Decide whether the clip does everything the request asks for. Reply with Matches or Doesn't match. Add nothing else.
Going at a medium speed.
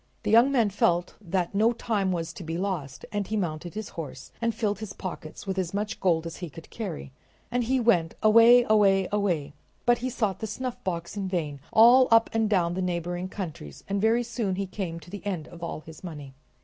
Doesn't match